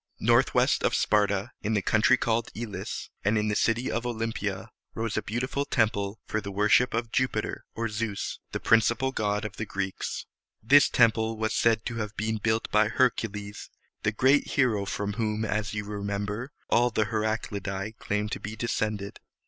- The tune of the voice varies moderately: No, narrow, 1.9 semitones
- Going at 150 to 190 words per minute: Yes, average, 180 wpm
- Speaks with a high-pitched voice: No, low, 110 Hz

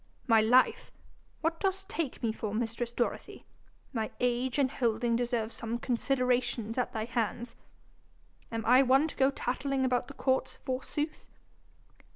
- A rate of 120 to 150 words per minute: Yes, average, 145 wpm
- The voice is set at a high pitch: Yes, high, 245 Hz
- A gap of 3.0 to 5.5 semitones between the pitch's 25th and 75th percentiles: No, narrow, 2.4 semitones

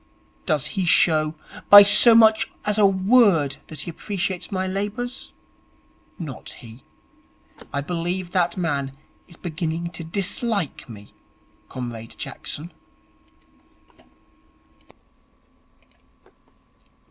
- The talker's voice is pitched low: No, medium, 175 Hz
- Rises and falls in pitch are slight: No, average, 4.7 semitones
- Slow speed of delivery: Yes, slow, 95 wpm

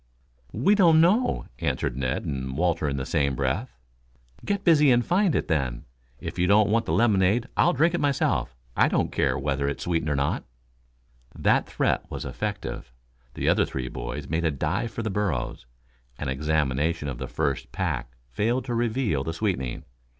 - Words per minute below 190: Yes, average, 180 wpm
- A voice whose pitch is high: No, very low, 85 Hz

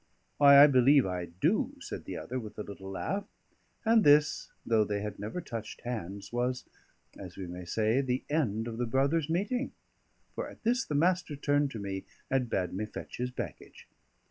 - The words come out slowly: No, average, 190 wpm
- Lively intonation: Yes, wide, 6.1 semitones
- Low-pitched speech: Yes, low, 125 Hz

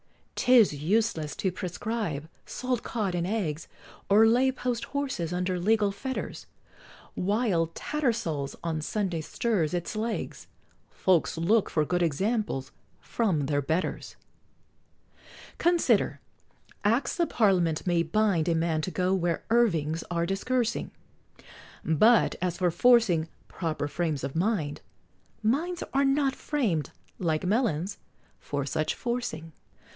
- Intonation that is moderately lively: No, wide, 6.0 semitones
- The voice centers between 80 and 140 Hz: No, medium, 185 Hz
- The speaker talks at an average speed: No, slow, 120 wpm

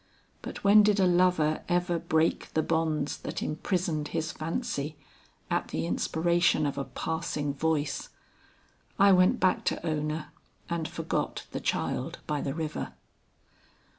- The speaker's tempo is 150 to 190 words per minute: No, slow, 135 wpm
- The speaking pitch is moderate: Yes, medium, 160 Hz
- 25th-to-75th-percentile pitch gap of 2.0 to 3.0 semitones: Yes, average, 2.7 semitones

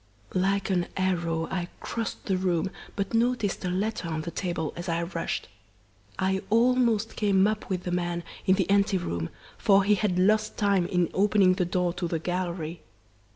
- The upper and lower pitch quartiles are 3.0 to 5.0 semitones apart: No, narrow, 2.6 semitones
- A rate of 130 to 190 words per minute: Yes, average, 180 wpm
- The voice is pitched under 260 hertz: Yes, medium, 185 Hz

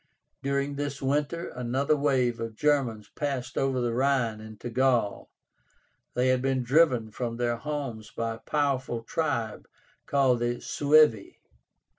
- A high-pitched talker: No, low, 130 Hz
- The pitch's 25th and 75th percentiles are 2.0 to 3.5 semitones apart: Yes, average, 3.2 semitones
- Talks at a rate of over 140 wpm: No, slow, 135 wpm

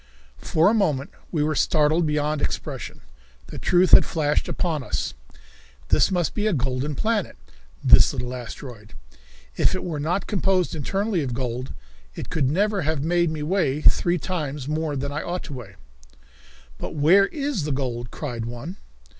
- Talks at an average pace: Yes, average, 165 wpm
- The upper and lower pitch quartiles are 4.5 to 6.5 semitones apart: Yes, average, 4.8 semitones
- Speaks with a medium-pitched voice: Yes, medium, 150 Hz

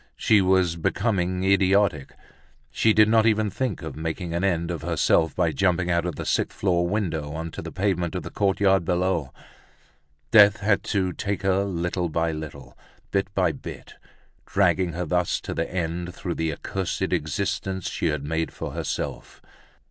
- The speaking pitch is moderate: No, very low, 90 Hz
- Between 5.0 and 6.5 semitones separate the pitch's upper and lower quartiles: No, average, 2.9 semitones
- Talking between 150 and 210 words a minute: Yes, average, 170 wpm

